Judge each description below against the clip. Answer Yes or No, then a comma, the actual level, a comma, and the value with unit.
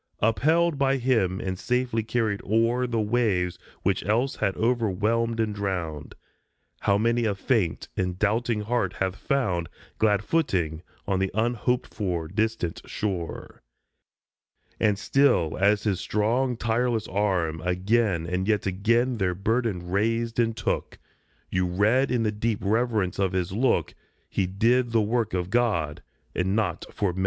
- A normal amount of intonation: Yes, average, 3.9 semitones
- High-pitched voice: No, low, 105 Hz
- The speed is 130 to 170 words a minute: Yes, average, 150 wpm